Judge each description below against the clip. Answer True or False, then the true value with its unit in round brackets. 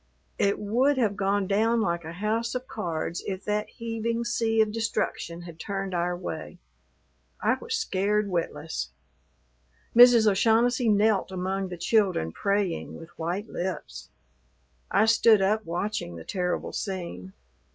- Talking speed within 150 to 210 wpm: False (140 wpm)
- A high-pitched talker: True (200 Hz)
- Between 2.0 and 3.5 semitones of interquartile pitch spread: False (3.9 semitones)